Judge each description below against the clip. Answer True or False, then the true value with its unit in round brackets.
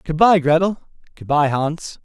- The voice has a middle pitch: True (160 Hz)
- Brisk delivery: False (120 wpm)